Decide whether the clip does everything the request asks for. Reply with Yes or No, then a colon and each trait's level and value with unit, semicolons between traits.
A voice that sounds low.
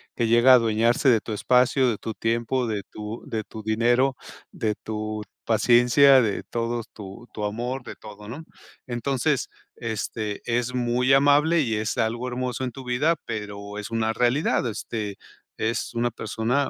Yes: low, 115 Hz